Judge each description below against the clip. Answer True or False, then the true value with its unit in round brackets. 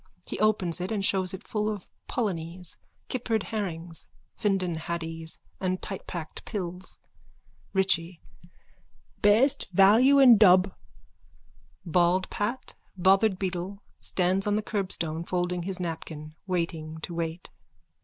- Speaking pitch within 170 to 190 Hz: True (185 Hz)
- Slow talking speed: True (115 wpm)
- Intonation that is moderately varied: True (3.2 semitones)